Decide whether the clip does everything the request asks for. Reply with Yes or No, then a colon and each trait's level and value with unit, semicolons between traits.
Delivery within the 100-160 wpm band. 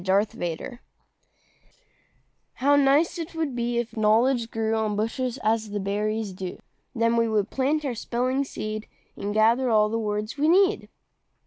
Yes: average, 150 wpm